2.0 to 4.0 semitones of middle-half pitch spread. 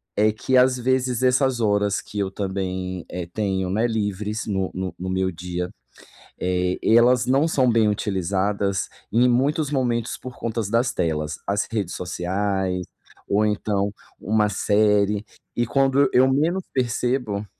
No: average, 4.5 semitones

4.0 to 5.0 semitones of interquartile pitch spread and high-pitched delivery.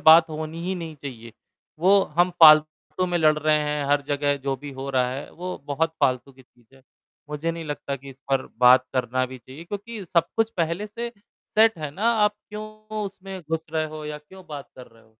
No: average, 4.3 semitones; medium, 155 Hz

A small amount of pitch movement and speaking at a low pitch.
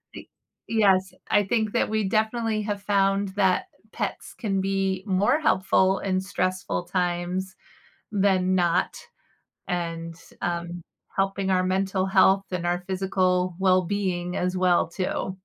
No: narrow, 1.4 semitones; high, 190 Hz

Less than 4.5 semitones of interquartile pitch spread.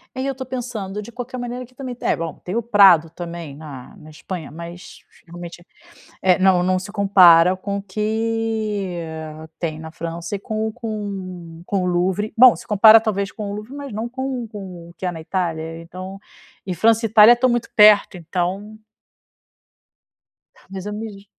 Yes: average, 4.1 semitones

